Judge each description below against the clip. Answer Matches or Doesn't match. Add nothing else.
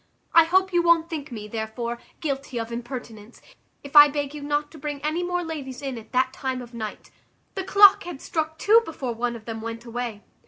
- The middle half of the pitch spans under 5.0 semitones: Doesn't match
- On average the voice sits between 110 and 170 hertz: Doesn't match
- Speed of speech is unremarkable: Doesn't match